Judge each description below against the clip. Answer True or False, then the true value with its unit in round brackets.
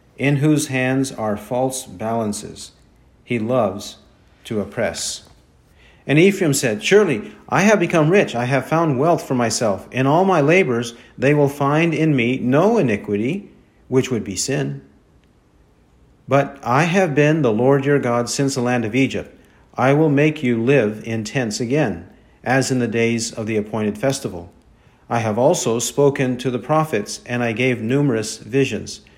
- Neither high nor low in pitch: False (130 Hz)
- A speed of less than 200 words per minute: True (165 wpm)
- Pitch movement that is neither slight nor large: True (4.0 semitones)